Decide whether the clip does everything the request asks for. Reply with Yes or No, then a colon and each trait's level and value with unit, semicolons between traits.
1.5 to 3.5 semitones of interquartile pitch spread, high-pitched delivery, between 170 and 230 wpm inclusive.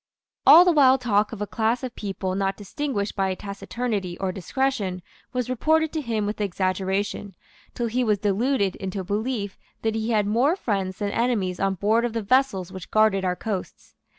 No: average, 4.0 semitones; high, 210 Hz; average, 185 wpm